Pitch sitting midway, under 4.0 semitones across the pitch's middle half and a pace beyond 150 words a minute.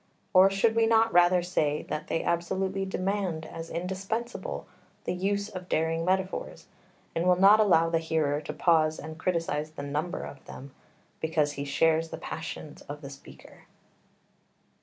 Yes: medium, 170 Hz; average, 3.4 semitones; average, 160 wpm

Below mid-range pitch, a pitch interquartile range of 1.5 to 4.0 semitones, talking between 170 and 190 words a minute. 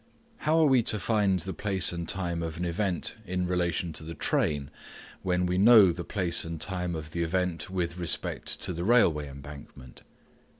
Yes: very low, 90 Hz; narrow, 2.4 semitones; average, 185 wpm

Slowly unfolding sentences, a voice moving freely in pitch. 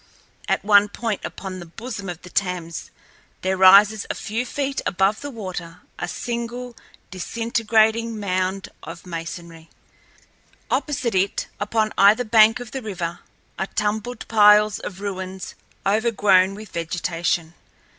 No: slow, 130 wpm; average, 3.5 semitones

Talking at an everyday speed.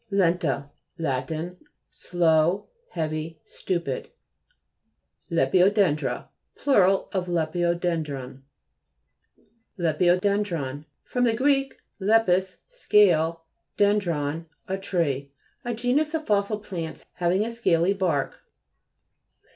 No: slow, 85 wpm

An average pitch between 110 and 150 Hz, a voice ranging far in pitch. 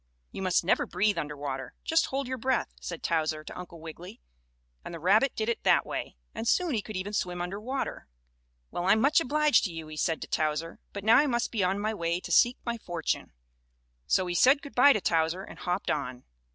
No: high, 190 Hz; wide, 6.2 semitones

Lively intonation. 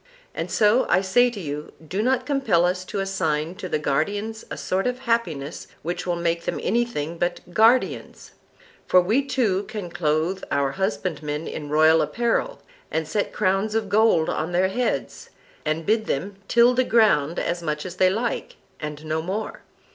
Yes: wide, 5.8 semitones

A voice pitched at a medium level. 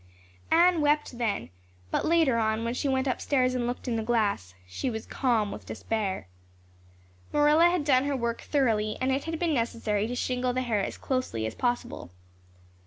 No: high, 245 Hz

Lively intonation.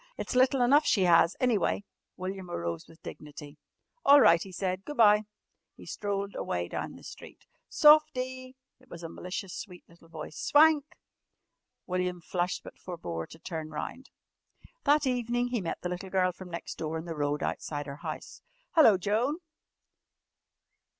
Yes: wide, 7.1 semitones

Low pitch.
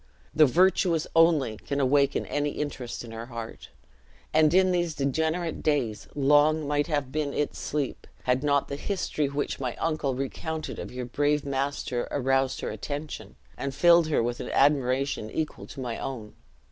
No: medium, 145 Hz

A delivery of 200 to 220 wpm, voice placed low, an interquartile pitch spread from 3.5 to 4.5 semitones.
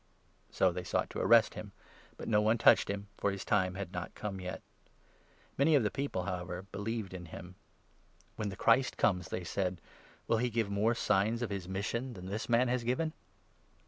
Yes: fast, 205 wpm; low, 100 Hz; average, 3.9 semitones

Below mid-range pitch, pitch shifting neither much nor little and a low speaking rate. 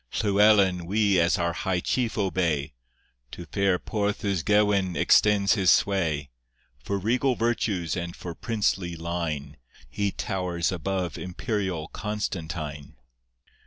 Yes: very low, 95 Hz; average, 3.3 semitones; slow, 115 wpm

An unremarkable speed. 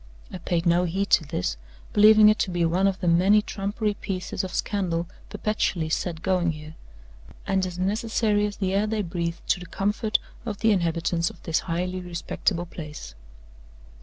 Yes: average, 175 wpm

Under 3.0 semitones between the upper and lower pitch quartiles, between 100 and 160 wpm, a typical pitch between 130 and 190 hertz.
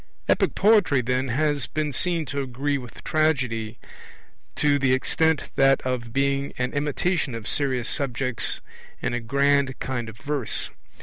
Yes: narrow, 2.6 semitones; average, 145 wpm; low, 135 Hz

